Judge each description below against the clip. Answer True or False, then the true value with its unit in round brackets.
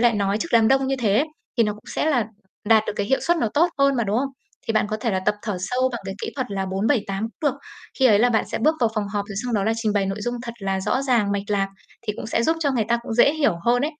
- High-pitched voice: True (225 Hz)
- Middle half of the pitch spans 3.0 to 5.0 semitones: True (4.0 semitones)